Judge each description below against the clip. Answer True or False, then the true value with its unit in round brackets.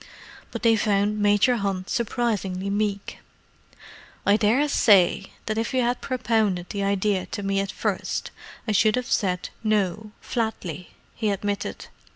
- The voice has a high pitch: True (205 Hz)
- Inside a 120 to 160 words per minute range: True (140 wpm)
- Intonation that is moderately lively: False (2.1 semitones)